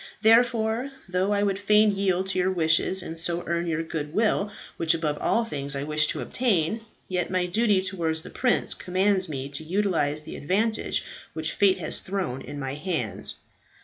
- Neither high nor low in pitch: Yes, medium, 180 Hz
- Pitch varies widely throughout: No, average, 4.3 semitones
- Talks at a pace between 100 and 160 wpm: No, average, 180 wpm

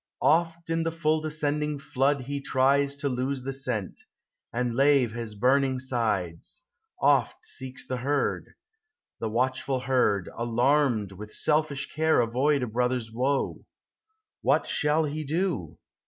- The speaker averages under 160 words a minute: Yes, average, 140 wpm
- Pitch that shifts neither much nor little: Yes, average, 3.5 semitones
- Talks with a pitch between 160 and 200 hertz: No, low, 135 Hz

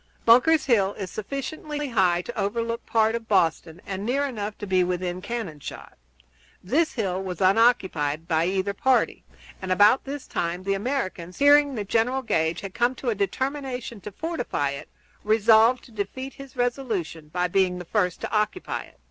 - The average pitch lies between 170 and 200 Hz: No, high, 210 Hz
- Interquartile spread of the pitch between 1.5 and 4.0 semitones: No, average, 5.3 semitones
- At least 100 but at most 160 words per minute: No, average, 175 wpm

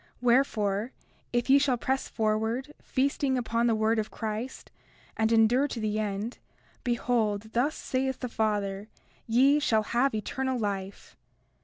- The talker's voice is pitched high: Yes, high, 230 Hz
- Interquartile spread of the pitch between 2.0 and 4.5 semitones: Yes, average, 3.3 semitones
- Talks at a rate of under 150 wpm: Yes, average, 140 wpm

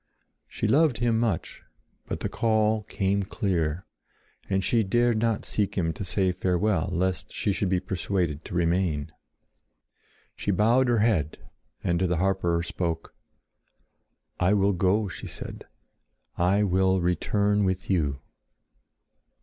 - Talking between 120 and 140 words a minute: Yes, slow, 135 wpm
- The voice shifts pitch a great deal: No, average, 3.0 semitones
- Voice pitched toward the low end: Yes, very low, 95 Hz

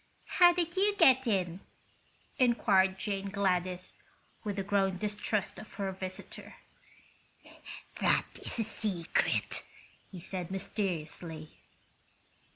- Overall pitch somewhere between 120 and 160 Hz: No, high, 195 Hz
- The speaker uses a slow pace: Yes, slow, 105 wpm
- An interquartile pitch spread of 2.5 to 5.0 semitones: Yes, average, 2.8 semitones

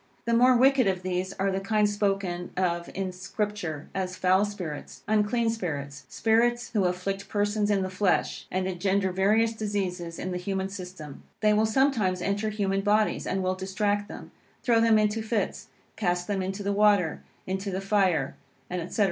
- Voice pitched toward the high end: Yes, high, 195 Hz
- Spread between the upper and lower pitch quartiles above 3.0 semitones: No, narrow, 2.4 semitones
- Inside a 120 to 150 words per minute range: No, average, 175 wpm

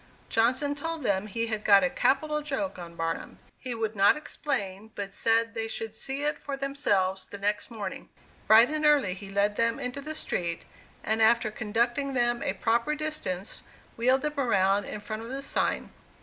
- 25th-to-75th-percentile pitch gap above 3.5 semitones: Yes, wide, 5.4 semitones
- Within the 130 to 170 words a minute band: No, average, 185 wpm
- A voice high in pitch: Yes, high, 230 Hz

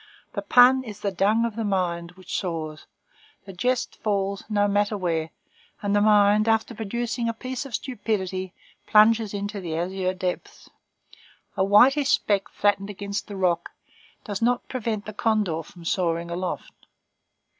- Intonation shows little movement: No, average, 3.2 semitones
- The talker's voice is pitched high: Yes, high, 205 Hz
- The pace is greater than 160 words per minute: No, average, 155 wpm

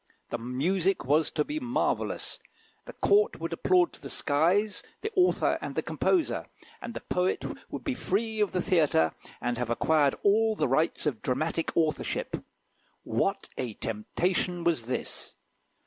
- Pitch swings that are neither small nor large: No, wide, 8.0 semitones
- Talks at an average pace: Yes, average, 155 wpm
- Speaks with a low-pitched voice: No, medium, 170 Hz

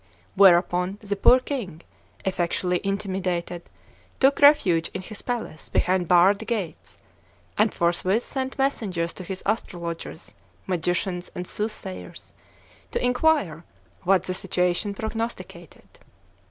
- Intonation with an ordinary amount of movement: Yes, average, 3.8 semitones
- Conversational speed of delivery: No, slow, 110 wpm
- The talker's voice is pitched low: No, high, 190 Hz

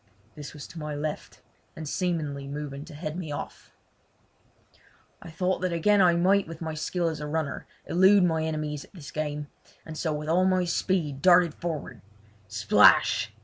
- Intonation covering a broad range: No, average, 3.0 semitones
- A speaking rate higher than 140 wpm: Yes, average, 175 wpm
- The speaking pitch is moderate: Yes, medium, 160 Hz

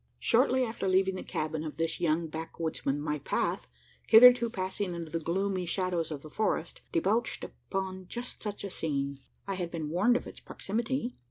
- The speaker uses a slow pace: No, average, 175 wpm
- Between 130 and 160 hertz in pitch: No, medium, 185 Hz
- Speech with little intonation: No, average, 4.5 semitones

